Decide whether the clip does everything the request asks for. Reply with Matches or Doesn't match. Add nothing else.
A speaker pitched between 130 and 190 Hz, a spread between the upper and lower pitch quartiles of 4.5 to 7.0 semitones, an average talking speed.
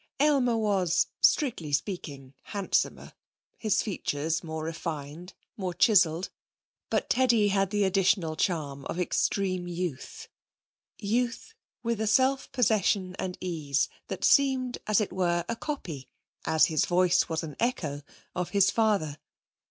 Doesn't match